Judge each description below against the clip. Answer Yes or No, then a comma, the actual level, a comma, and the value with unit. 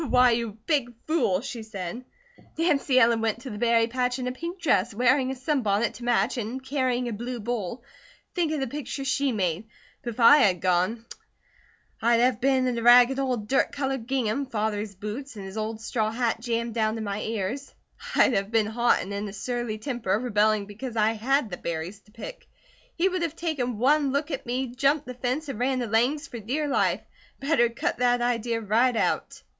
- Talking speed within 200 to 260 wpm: Yes, fast, 205 wpm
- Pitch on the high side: Yes, high, 240 Hz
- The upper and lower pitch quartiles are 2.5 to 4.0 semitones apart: Yes, average, 3.4 semitones